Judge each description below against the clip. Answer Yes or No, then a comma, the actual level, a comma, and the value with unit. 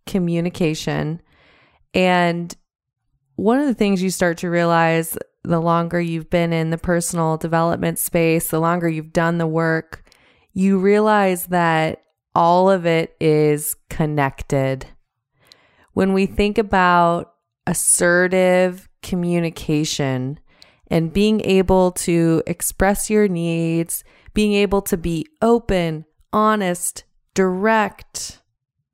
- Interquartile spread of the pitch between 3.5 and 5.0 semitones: No, average, 2.7 semitones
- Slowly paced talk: Yes, slow, 110 wpm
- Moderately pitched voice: Yes, medium, 170 Hz